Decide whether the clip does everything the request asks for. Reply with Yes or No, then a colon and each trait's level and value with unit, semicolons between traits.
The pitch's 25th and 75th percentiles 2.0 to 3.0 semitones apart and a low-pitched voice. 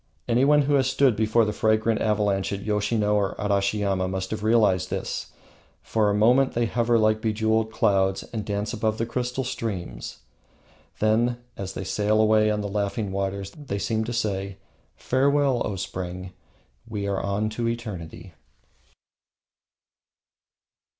Yes: average, 2.7 semitones; low, 110 Hz